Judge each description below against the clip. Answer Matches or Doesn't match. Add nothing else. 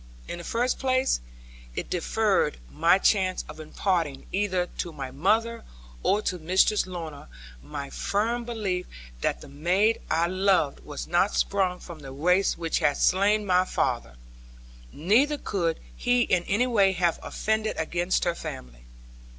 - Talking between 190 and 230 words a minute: Doesn't match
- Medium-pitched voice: Matches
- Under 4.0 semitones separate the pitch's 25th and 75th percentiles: Doesn't match